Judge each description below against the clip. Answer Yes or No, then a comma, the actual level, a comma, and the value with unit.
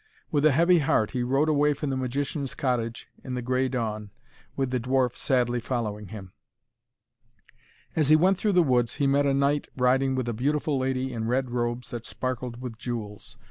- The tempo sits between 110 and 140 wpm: No, average, 190 wpm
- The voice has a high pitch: No, low, 130 Hz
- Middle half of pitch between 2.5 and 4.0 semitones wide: Yes, average, 2.8 semitones